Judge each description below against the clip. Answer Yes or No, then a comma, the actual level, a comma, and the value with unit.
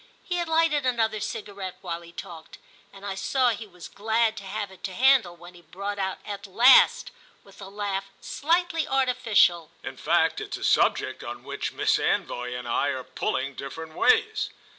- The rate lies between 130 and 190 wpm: Yes, average, 185 wpm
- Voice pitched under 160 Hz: No, high, 200 Hz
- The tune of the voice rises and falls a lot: Yes, wide, 5.7 semitones